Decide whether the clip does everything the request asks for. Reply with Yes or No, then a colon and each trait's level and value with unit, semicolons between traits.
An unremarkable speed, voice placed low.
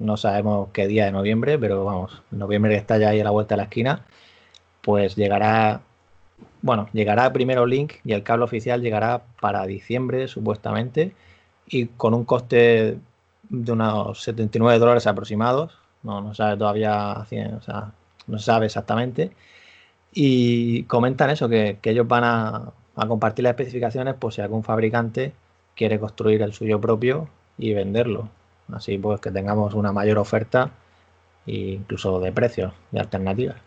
Yes: average, 155 wpm; low, 110 Hz